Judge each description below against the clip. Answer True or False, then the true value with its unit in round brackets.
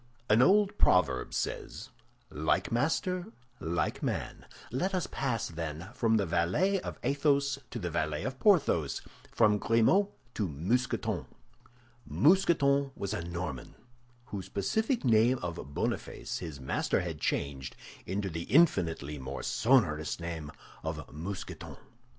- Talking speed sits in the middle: False (125 wpm)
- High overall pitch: False (100 Hz)